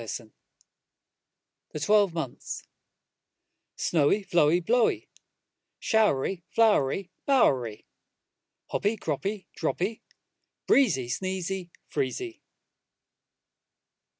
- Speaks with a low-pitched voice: No, medium, 180 Hz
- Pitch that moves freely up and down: Yes, wide, 6.7 semitones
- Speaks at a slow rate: Yes, slow, 70 wpm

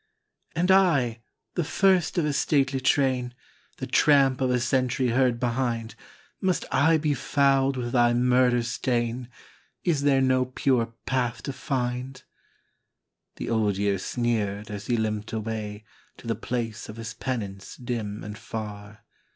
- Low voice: Yes, low, 125 Hz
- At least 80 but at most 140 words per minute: No, average, 150 wpm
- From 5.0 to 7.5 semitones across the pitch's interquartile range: No, average, 3.0 semitones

